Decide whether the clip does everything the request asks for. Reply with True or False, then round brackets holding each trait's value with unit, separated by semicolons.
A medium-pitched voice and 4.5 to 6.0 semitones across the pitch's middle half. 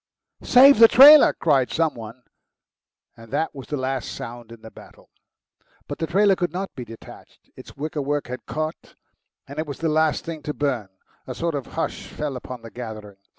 True (145 Hz; 5.0 semitones)